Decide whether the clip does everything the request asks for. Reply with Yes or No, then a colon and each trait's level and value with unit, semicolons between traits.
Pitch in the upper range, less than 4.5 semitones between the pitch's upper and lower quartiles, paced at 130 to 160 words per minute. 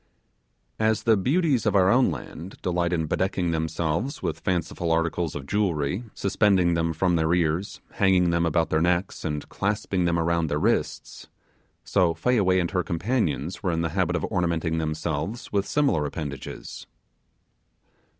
No: very low, 85 Hz; average, 3.3 semitones; average, 155 wpm